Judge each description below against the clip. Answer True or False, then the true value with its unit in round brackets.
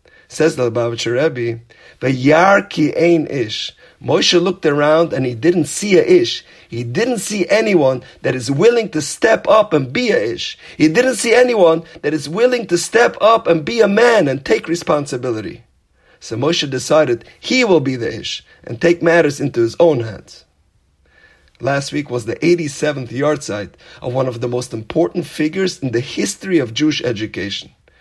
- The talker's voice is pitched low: False (155 Hz)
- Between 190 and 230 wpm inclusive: False (180 wpm)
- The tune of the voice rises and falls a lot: True (6.5 semitones)